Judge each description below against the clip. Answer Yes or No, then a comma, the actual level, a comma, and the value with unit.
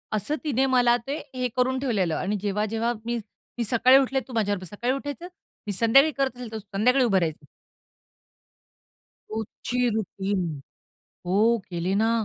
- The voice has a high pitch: Yes, high, 235 Hz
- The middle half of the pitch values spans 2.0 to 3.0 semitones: No, average, 4.2 semitones